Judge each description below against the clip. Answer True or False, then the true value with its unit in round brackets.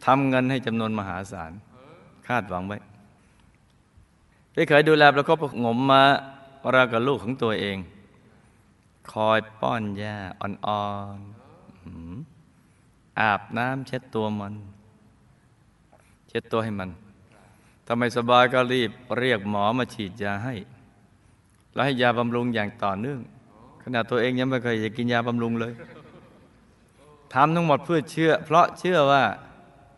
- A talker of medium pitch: False (115 Hz)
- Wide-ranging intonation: False (3.7 semitones)